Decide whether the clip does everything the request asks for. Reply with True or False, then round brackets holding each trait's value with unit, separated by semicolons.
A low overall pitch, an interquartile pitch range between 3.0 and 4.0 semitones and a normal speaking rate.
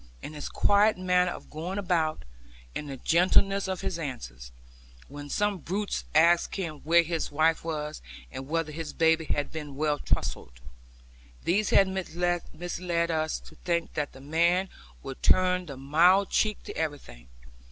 False (165 Hz; 3.4 semitones; 155 wpm)